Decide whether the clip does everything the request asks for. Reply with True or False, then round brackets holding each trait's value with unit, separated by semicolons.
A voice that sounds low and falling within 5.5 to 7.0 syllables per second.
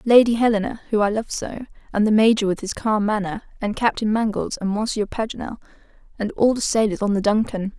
False (215 Hz; 5.8 syllables/s)